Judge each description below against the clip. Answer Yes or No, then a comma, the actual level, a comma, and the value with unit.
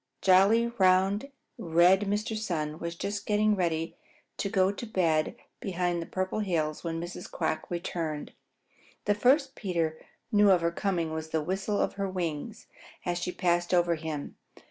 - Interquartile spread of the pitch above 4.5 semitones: No, average, 3.2 semitones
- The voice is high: No, medium, 180 Hz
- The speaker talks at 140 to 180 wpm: Yes, average, 160 wpm